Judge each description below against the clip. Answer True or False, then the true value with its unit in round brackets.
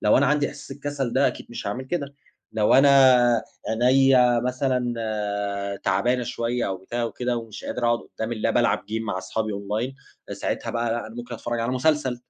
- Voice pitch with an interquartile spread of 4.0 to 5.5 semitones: False (2.9 semitones)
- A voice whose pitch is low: True (120 Hz)